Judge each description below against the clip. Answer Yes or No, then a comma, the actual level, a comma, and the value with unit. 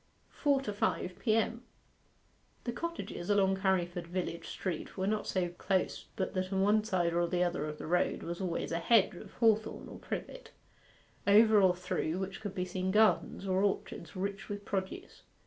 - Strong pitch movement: No, average, 2.8 semitones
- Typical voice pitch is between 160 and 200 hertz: Yes, high, 190 Hz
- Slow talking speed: No, average, 175 wpm